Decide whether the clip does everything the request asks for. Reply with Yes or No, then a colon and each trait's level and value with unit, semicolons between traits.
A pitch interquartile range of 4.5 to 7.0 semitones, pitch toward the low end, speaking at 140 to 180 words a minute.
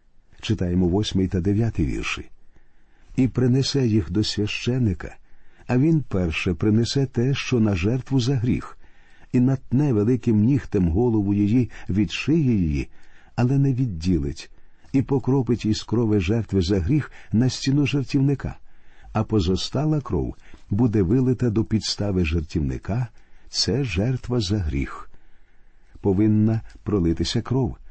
No: average, 5.2 semitones; low, 110 Hz; average, 120 wpm